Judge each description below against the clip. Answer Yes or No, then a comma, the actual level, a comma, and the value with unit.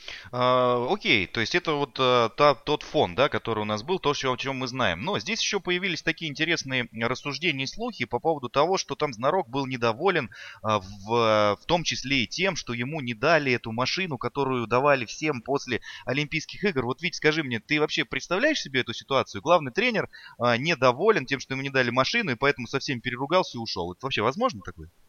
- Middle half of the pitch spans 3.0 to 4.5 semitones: No, average, 4.9 semitones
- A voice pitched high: No, low, 135 Hz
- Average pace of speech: No, fast, 210 wpm